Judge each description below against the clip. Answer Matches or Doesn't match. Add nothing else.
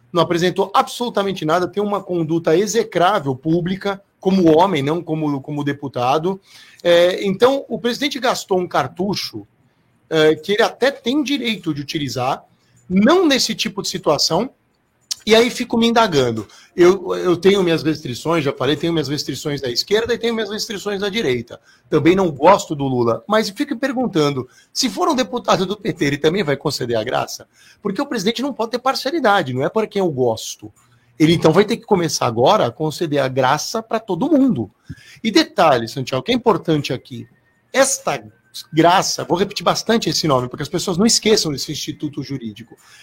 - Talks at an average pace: Matches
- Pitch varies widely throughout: Matches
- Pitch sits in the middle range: Matches